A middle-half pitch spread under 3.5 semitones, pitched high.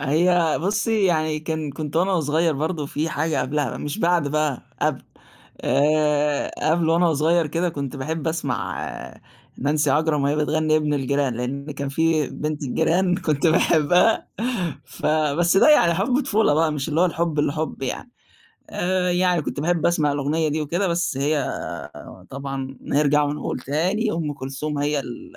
No: average, 2.8 semitones; medium, 155 Hz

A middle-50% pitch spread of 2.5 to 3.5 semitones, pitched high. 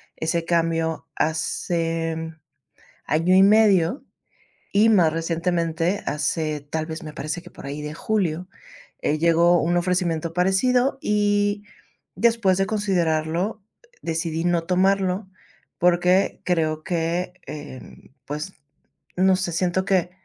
No: average, 2.8 semitones; medium, 175 Hz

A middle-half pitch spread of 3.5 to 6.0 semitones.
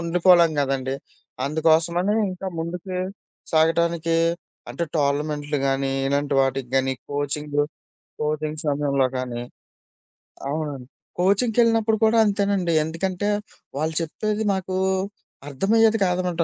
Yes: average, 4.4 semitones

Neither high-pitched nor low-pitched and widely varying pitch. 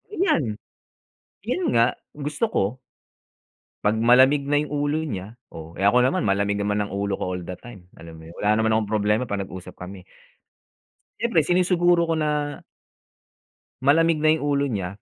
No: low, 120 Hz; wide, 7.0 semitones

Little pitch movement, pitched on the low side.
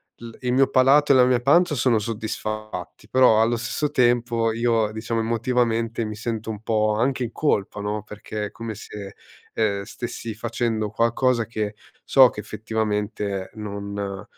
Yes: narrow, 2.2 semitones; low, 115 Hz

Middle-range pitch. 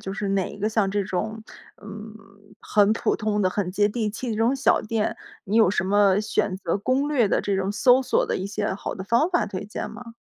No: high, 210 Hz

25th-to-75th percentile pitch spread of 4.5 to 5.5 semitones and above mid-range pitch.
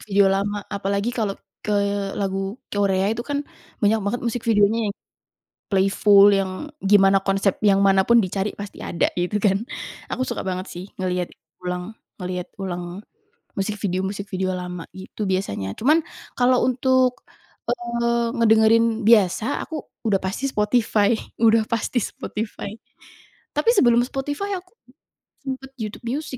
No: average, 3.5 semitones; high, 205 Hz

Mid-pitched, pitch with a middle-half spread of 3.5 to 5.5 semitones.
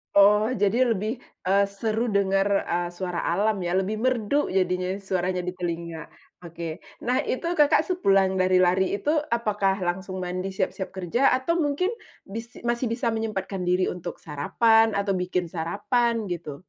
No: high, 195 Hz; average, 4.1 semitones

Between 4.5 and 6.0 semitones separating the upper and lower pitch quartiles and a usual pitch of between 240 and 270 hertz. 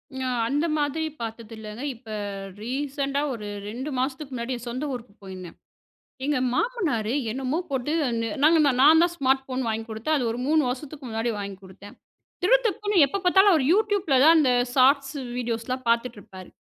Yes: average, 4.8 semitones; very high, 260 Hz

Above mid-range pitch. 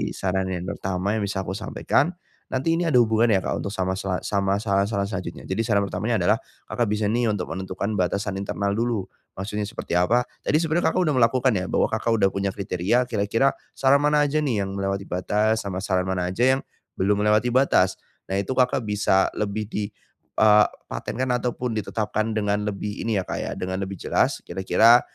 No: low, 105 Hz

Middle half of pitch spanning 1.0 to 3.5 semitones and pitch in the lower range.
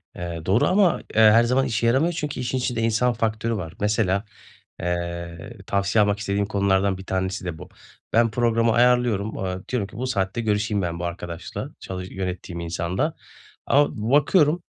No: average, 4.3 semitones; low, 105 Hz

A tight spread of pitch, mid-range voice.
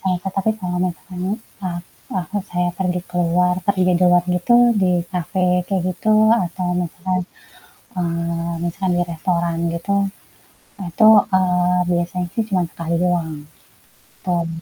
Yes: narrow, 1.2 semitones; medium, 180 Hz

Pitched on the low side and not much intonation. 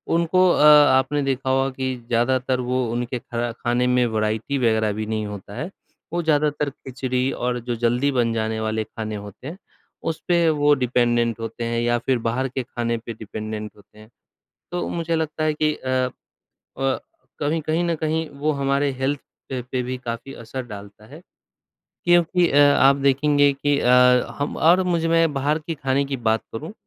No: low, 130 Hz; average, 3.9 semitones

